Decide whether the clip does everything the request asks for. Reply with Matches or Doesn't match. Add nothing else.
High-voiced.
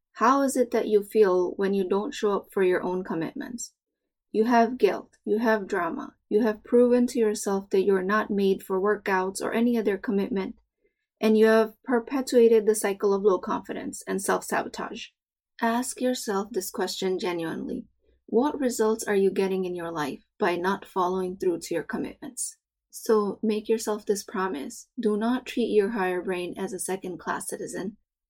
Matches